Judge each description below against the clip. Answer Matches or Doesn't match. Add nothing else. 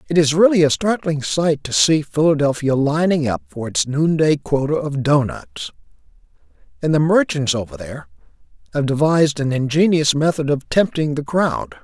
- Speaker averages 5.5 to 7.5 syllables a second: Doesn't match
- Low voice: Doesn't match